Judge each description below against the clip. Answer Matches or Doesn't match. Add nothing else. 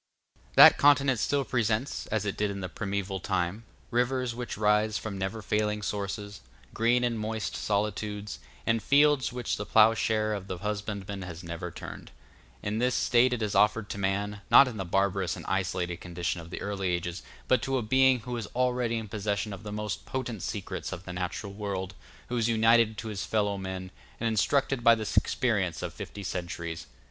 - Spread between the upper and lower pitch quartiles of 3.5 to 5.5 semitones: Doesn't match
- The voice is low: Matches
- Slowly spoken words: Doesn't match